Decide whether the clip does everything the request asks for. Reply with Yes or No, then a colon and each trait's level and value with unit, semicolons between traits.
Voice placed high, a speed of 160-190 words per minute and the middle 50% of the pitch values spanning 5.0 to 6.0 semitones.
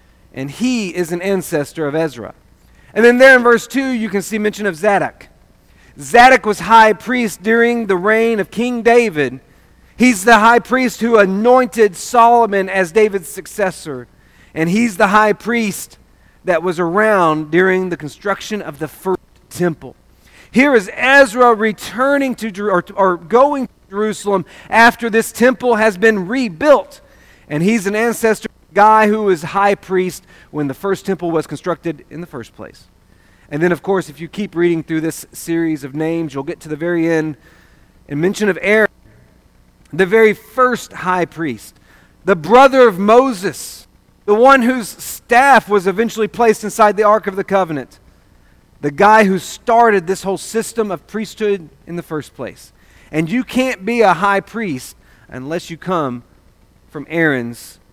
Yes: high, 195 Hz; average, 165 wpm; wide, 5.6 semitones